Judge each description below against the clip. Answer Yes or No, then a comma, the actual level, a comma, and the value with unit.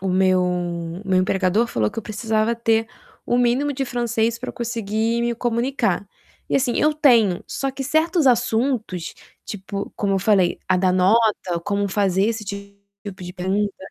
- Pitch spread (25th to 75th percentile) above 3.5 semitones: Yes, average, 3.9 semitones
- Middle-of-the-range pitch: No, high, 215 Hz